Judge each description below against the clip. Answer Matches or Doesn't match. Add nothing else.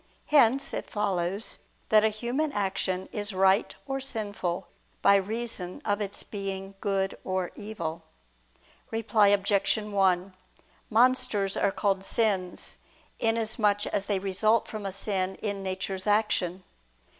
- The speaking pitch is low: Doesn't match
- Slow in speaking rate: Matches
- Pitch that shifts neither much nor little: Doesn't match